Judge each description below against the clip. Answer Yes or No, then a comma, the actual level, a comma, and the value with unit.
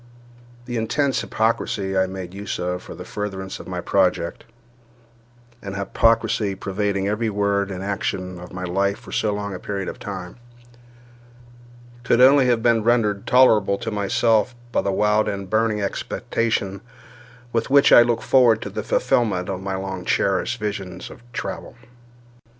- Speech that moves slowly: No, average, 150 wpm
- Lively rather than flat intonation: No, average, 3.6 semitones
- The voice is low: Yes, low, 105 Hz